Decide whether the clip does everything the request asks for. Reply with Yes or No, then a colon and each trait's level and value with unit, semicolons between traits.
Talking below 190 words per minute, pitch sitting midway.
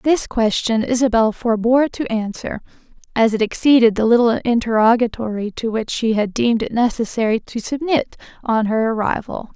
No: average, 150 wpm; high, 230 Hz